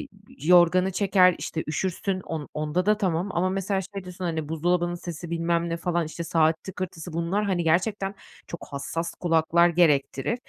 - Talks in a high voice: No, medium, 175 Hz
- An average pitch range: No, narrow, 2.3 semitones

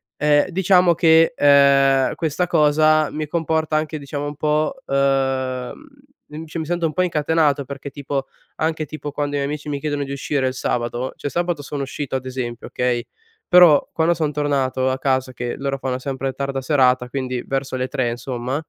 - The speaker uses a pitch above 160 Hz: No, medium, 140 Hz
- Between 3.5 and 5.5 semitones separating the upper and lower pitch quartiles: No, average, 2.8 semitones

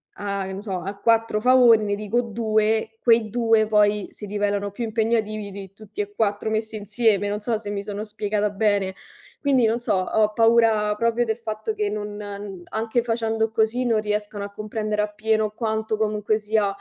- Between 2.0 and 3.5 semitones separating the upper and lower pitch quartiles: No, narrow, 1.3 semitones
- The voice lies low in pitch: No, high, 215 Hz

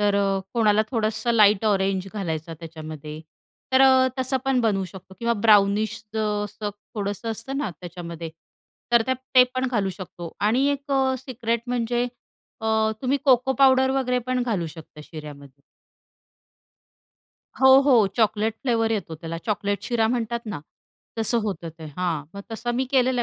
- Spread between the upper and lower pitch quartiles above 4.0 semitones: Yes, average, 4.7 semitones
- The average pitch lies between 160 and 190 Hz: No, high, 220 Hz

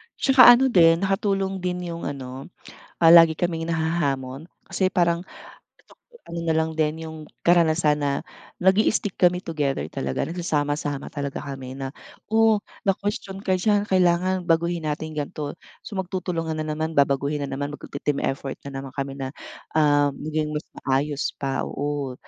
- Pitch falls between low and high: Yes, medium, 160 Hz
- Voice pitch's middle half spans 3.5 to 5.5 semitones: Yes, average, 3.9 semitones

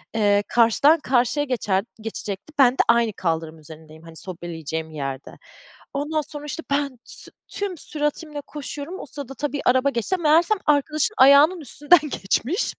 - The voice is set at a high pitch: Yes, very high, 270 Hz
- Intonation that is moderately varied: No, wide, 7.4 semitones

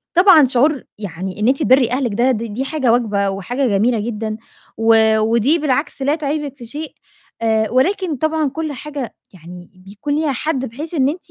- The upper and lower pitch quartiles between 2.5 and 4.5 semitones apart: No, average, 5.1 semitones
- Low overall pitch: No, very high, 255 Hz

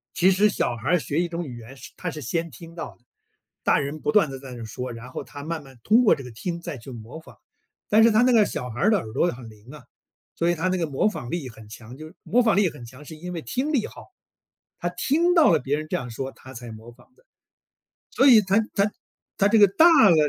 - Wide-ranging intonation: Yes, wide, 8.1 semitones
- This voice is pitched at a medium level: Yes, medium, 160 Hz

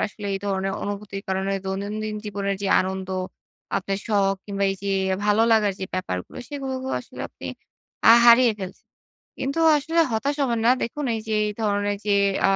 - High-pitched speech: Yes, high, 205 Hz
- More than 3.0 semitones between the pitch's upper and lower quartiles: No, average, 2.7 semitones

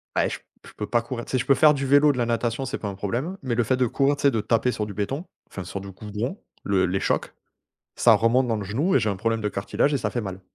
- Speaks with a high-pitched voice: No, low, 115 Hz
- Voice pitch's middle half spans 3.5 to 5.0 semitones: Yes, average, 4.4 semitones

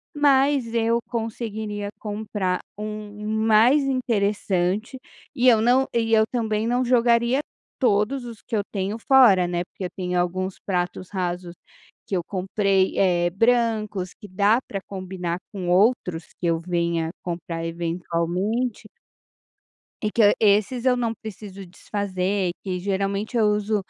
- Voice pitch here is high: Yes, high, 205 Hz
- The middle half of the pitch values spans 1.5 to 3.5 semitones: No, average, 3.9 semitones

